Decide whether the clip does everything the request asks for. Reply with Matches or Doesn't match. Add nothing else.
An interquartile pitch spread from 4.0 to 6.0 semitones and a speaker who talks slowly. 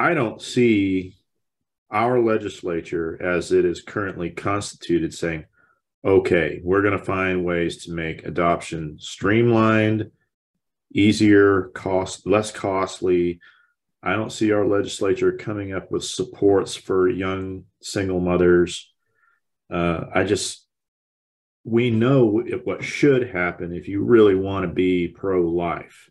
Doesn't match